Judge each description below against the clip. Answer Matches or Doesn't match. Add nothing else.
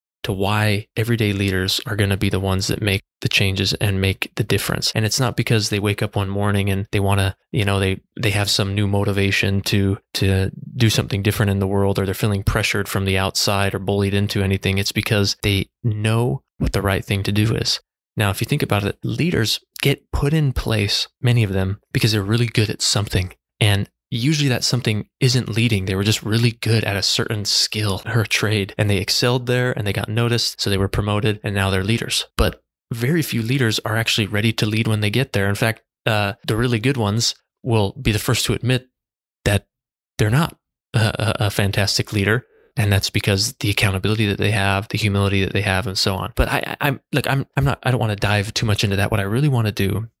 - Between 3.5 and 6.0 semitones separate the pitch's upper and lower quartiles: Doesn't match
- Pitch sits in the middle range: Doesn't match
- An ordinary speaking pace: Doesn't match